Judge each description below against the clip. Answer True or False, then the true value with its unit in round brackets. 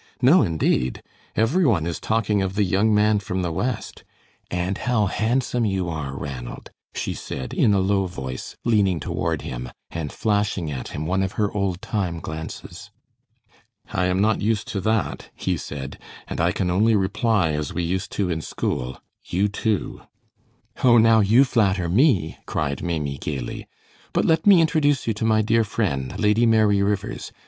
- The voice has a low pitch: True (100 Hz)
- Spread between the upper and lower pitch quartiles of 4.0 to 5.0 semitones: True (4.7 semitones)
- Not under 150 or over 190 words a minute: True (175 wpm)